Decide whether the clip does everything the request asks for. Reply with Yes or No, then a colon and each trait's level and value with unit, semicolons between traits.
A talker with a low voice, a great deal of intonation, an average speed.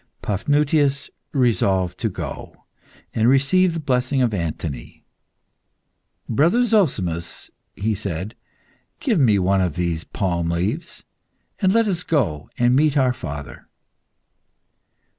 No: low, 120 Hz; wide, 8.4 semitones; slow, 115 wpm